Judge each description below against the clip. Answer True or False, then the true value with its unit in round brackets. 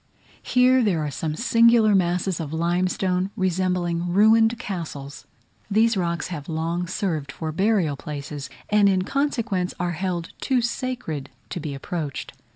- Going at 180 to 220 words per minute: False (140 wpm)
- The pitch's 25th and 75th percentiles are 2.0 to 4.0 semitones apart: False (4.8 semitones)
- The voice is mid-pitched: True (180 Hz)